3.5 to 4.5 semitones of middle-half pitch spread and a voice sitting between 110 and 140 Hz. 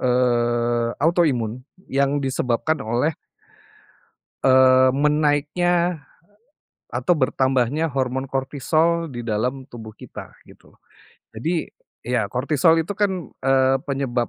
Yes: average, 3.9 semitones; low, 135 Hz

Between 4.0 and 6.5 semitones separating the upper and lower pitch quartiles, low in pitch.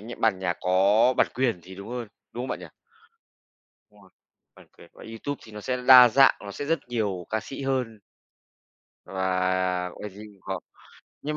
Yes: average, 4.9 semitones; low, 110 Hz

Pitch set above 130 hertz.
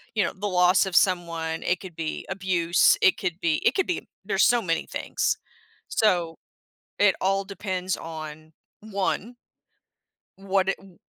Yes: medium, 185 Hz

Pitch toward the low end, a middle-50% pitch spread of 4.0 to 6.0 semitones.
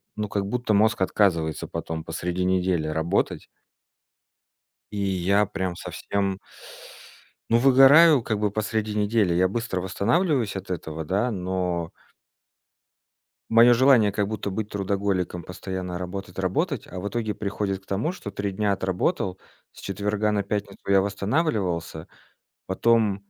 No: low, 100 Hz; narrow, 2.6 semitones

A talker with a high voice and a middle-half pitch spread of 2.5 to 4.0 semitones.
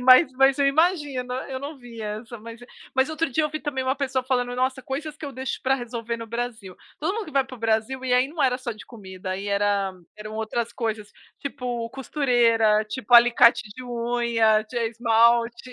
Yes: high, 245 Hz; average, 2.8 semitones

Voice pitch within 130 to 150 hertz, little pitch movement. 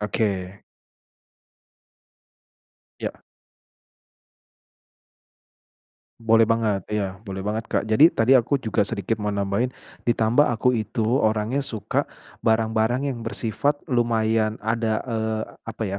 No: low, 110 Hz; narrow, 1.7 semitones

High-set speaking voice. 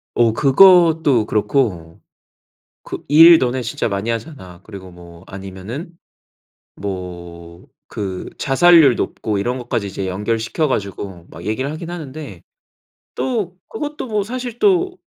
No: low, 120 Hz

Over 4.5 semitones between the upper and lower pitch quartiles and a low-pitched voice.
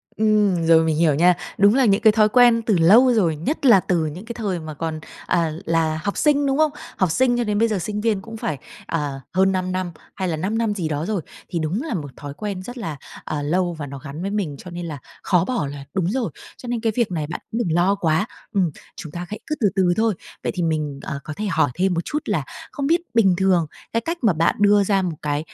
No: average, 5.1 semitones; medium, 185 Hz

